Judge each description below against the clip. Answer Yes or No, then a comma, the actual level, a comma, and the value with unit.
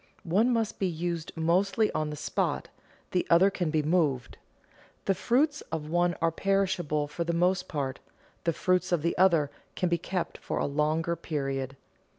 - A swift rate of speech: No, average, 170 wpm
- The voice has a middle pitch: Yes, medium, 170 Hz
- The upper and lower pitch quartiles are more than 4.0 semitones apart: No, average, 3.4 semitones